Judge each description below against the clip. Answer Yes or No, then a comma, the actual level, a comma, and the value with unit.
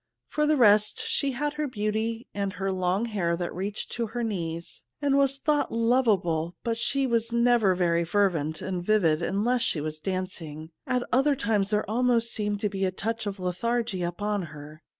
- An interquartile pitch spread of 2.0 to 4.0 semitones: No, average, 4.8 semitones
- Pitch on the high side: Yes, high, 210 Hz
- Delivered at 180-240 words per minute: Yes, average, 185 wpm